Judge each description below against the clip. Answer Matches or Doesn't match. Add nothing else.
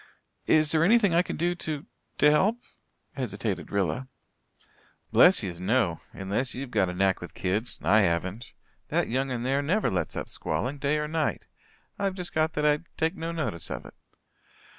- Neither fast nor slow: Matches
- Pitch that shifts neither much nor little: Doesn't match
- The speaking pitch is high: Doesn't match